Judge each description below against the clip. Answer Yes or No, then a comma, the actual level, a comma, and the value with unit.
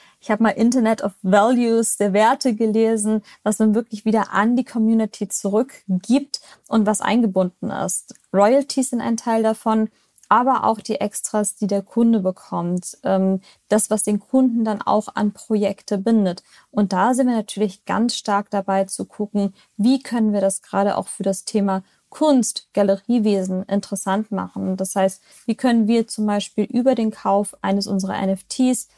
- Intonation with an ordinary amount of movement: No, narrow, 2.3 semitones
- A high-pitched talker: Yes, high, 210 Hz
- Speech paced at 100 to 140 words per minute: No, average, 165 wpm